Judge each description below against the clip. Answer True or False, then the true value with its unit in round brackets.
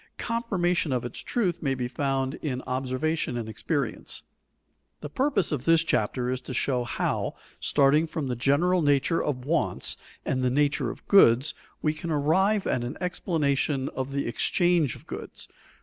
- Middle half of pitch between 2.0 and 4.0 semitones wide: False (4.4 semitones)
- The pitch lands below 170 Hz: True (140 Hz)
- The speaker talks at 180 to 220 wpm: False (165 wpm)